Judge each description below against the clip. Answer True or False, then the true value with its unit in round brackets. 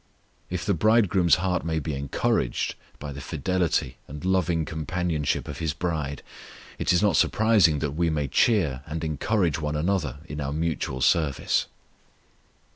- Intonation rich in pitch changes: False (3.7 semitones)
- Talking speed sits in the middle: True (150 wpm)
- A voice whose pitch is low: True (80 Hz)